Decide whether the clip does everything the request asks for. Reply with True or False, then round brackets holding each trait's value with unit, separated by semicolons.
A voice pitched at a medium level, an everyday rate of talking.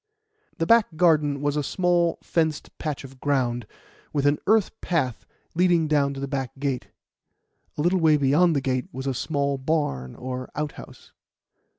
True (145 Hz; 165 wpm)